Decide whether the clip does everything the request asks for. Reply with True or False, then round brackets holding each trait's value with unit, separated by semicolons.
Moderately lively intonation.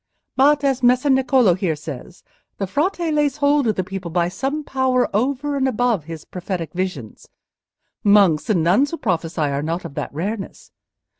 False (7.9 semitones)